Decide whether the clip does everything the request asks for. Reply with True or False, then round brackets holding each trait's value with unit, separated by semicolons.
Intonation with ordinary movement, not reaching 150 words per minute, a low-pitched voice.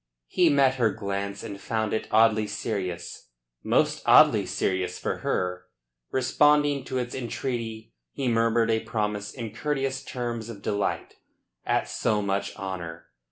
True (3.8 semitones; 140 wpm; 110 Hz)